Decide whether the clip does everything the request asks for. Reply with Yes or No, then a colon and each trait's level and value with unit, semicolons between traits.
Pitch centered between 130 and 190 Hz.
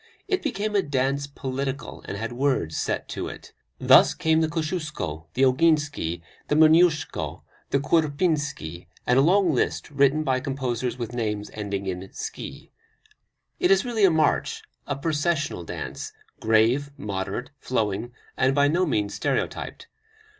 Yes: medium, 140 Hz